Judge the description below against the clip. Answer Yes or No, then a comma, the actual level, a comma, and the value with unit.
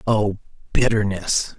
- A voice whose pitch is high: No, low, 100 Hz